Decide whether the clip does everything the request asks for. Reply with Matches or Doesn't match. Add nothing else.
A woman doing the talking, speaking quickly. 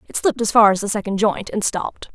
Matches